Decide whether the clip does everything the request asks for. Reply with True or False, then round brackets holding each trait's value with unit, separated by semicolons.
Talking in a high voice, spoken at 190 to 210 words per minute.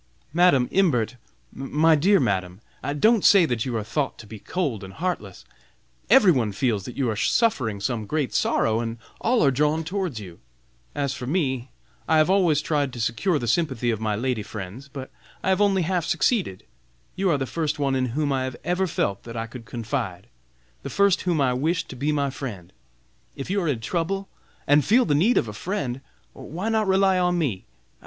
False (140 Hz; 200 wpm)